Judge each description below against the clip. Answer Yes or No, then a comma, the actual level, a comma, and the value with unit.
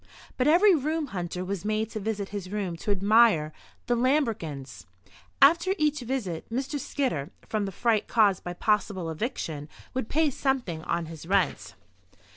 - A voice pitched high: Yes, high, 210 Hz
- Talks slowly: No, average, 155 wpm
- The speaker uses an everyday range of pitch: No, wide, 6.9 semitones